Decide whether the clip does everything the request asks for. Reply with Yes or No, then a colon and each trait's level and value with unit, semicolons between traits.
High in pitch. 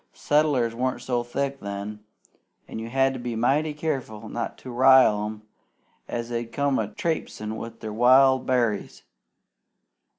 No: low, 125 Hz